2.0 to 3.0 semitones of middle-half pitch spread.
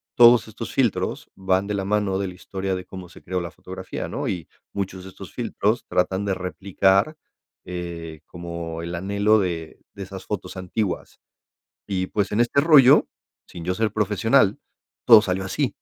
Yes: narrow, 2.5 semitones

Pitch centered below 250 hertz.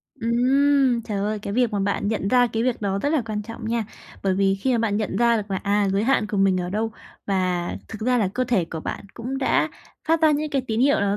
Yes: high, 220 Hz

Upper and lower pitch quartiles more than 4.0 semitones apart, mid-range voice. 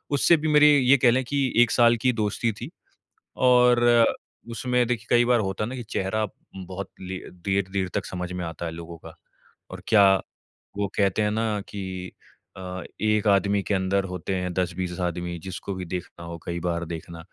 No: average, 4.4 semitones; very low, 95 Hz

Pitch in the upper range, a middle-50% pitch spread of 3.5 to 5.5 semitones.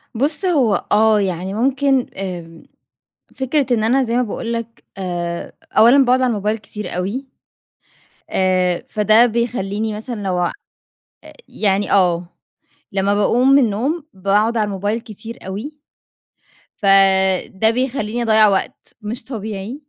Yes: high, 215 Hz; average, 3.9 semitones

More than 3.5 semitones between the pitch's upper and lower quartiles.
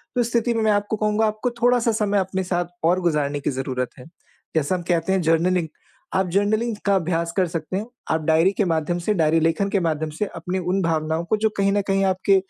Yes: average, 4.0 semitones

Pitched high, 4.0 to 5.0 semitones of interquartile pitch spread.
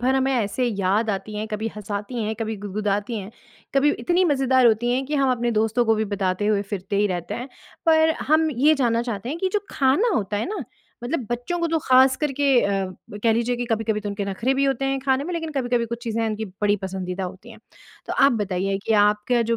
Yes: high, 230 Hz; average, 4.4 semitones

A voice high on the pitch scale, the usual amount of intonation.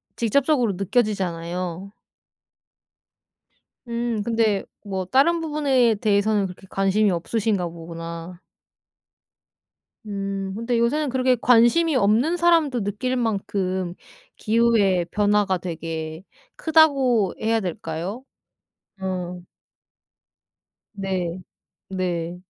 Yes: high, 205 Hz; average, 4.7 semitones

